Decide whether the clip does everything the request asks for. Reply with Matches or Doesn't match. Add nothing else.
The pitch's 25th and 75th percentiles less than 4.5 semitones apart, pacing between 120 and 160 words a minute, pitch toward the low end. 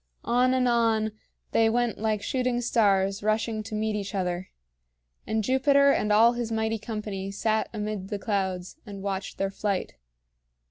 Doesn't match